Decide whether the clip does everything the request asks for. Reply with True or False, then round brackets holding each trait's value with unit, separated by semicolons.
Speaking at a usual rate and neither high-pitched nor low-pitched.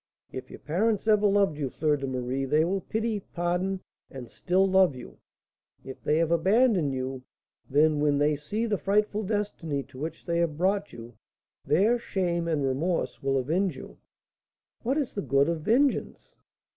True (170 wpm; 170 Hz)